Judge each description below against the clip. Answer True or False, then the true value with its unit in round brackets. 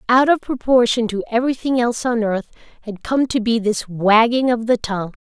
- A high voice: True (230 Hz)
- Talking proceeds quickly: False (195 wpm)